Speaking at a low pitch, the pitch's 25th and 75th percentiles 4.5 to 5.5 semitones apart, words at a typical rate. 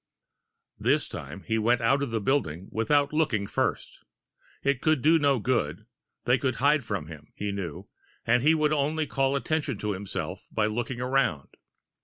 Yes: low, 125 Hz; average, 5.2 semitones; average, 170 wpm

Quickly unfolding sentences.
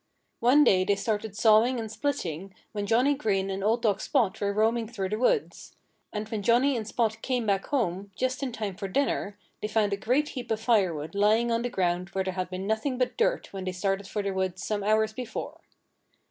Yes: fast, 215 wpm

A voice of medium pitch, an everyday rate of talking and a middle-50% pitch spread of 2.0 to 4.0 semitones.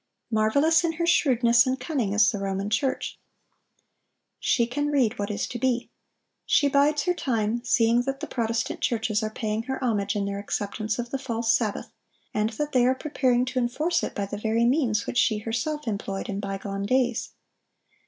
No: high, 235 Hz; average, 185 wpm; average, 3.7 semitones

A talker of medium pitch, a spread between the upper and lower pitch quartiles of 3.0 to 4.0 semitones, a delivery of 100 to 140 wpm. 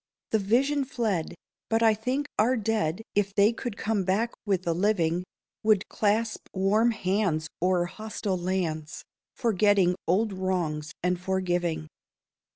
No: high, 195 Hz; average, 3.7 semitones; slow, 135 wpm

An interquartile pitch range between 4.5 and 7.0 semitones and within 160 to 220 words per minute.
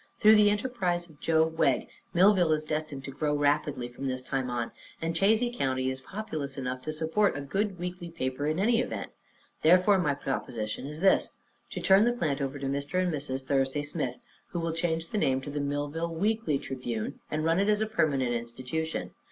Yes: average, 5.0 semitones; average, 200 wpm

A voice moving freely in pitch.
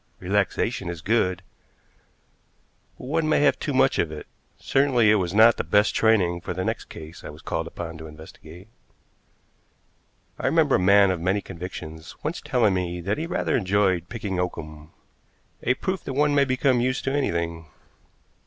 Yes: wide, 6.7 semitones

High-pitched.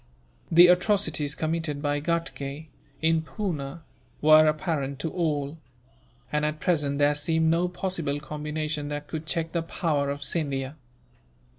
No: medium, 155 Hz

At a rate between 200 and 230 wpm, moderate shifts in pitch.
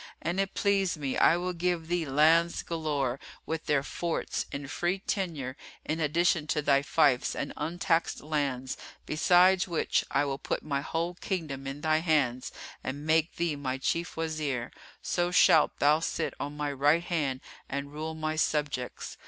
No: average, 165 wpm; average, 3.2 semitones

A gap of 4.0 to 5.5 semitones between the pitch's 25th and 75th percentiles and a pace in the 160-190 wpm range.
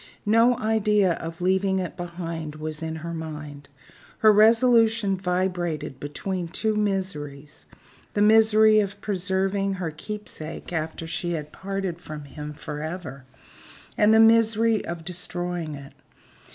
No: average, 4.8 semitones; slow, 135 wpm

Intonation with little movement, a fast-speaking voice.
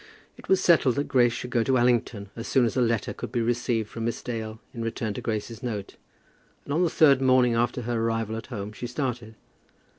Yes: narrow, 1.9 semitones; fast, 220 wpm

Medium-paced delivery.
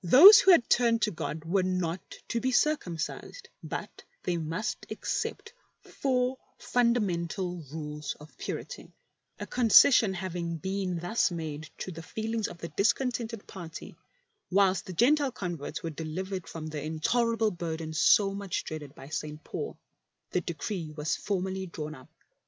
Yes: average, 150 wpm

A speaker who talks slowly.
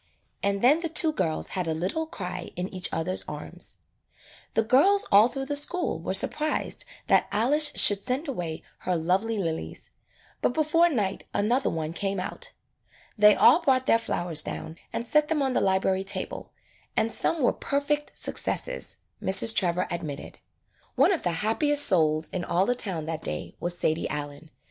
No: average, 175 wpm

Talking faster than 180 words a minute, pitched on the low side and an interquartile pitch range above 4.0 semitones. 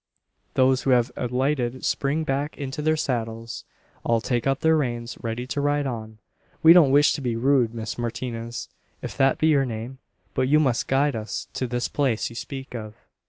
No: average, 190 wpm; low, 130 Hz; average, 3.2 semitones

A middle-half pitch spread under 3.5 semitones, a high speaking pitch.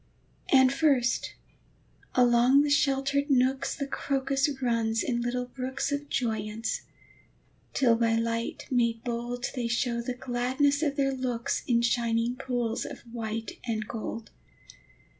Yes: narrow, 2.6 semitones; high, 245 Hz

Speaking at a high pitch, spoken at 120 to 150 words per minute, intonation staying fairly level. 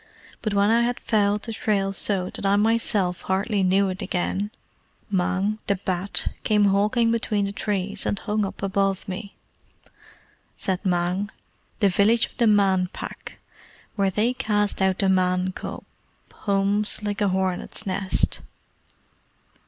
Yes: high, 200 Hz; average, 145 wpm; narrow, 1.8 semitones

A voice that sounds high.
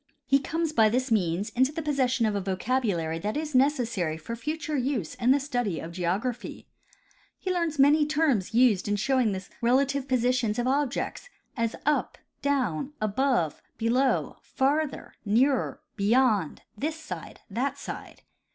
Yes: very high, 250 Hz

